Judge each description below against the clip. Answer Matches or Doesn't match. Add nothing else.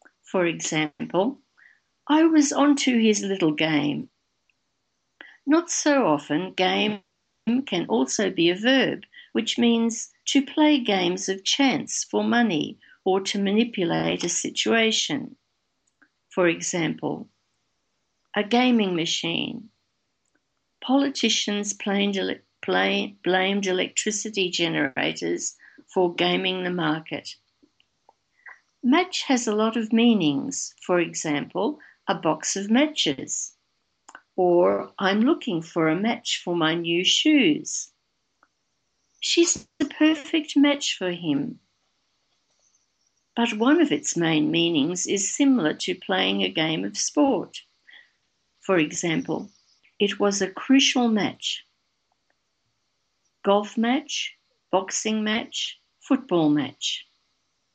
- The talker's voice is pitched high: Matches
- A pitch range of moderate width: Doesn't match